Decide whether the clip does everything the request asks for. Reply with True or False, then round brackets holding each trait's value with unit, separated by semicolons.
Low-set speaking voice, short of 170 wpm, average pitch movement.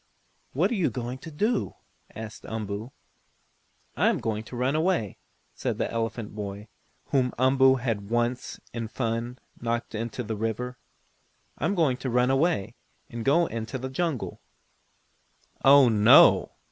True (120 Hz; 150 wpm; 3.0 semitones)